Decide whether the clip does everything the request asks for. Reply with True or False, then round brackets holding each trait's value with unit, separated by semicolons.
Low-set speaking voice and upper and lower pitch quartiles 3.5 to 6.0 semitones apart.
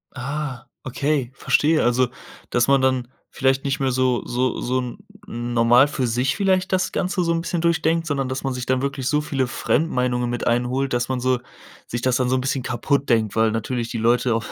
False (130 Hz; 2.5 semitones)